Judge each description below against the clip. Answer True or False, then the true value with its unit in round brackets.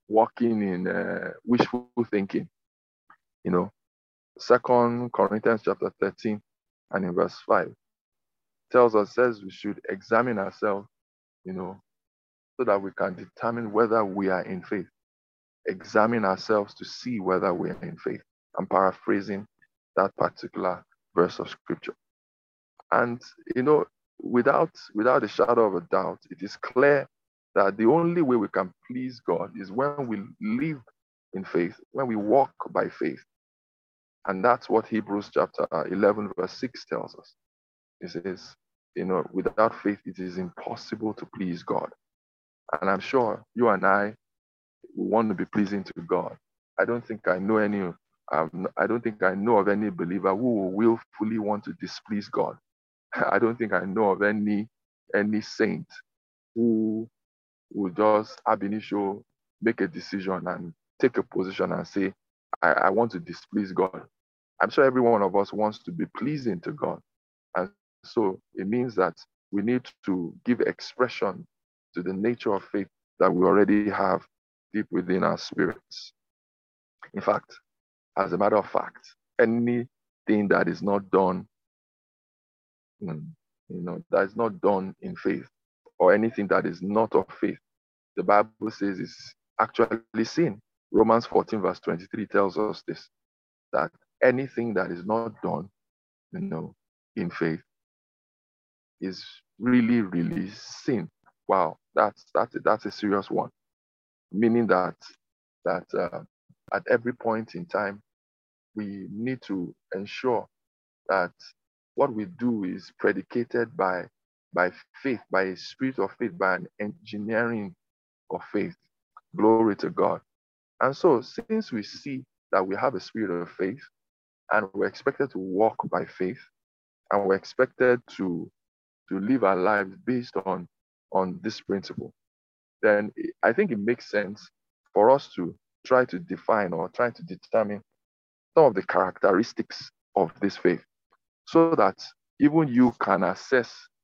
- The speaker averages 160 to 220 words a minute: False (150 wpm)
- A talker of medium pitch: False (105 Hz)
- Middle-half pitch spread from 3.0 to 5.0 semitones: True (4.2 semitones)